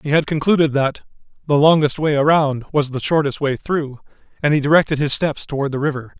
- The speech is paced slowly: No, fast, 205 wpm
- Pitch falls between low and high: Yes, medium, 145 Hz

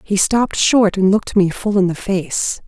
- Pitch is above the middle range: Yes, high, 200 Hz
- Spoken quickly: Yes, fast, 225 wpm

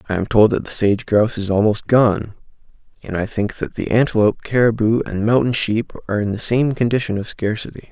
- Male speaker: Yes, male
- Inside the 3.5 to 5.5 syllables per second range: No, 5.8 syllables/s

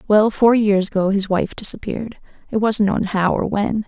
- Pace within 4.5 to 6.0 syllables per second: Yes, 5.0 syllables/s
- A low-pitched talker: No, high, 205 Hz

